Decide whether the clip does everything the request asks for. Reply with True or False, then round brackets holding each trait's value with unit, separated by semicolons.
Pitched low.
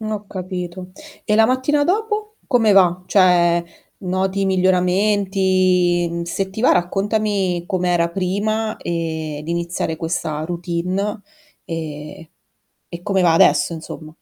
False (185 Hz)